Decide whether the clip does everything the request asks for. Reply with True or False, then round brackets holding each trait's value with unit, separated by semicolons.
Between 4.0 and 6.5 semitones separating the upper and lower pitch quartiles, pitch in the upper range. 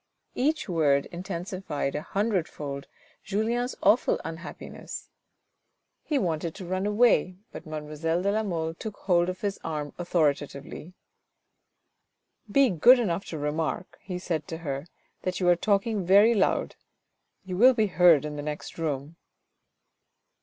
False (4.5 semitones; 175 Hz)